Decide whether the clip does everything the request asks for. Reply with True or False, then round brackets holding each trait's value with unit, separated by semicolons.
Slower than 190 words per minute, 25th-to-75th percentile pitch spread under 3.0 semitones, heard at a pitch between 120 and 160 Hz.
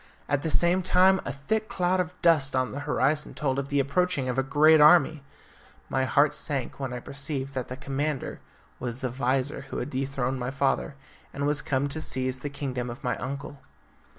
False (200 wpm; 2.6 semitones; 140 Hz)